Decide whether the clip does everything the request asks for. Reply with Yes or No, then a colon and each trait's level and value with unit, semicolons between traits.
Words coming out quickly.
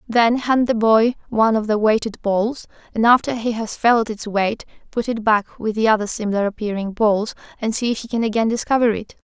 Yes: fast, 215 wpm